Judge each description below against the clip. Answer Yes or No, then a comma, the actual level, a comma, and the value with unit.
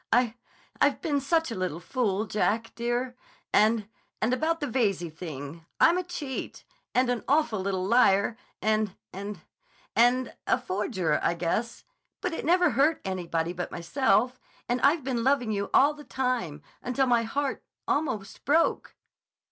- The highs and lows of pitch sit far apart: Yes, wide, 5.8 semitones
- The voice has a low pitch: No, high, 235 Hz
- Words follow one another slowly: Yes, slow, 125 wpm